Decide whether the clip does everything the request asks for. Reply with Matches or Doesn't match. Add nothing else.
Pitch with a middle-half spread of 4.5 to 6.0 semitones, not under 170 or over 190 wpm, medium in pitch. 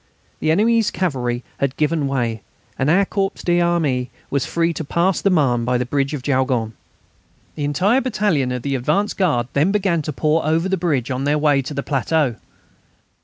Matches